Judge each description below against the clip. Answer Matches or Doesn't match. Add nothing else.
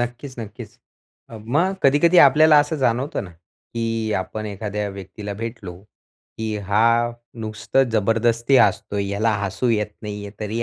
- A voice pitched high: Doesn't match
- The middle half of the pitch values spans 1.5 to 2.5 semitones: Doesn't match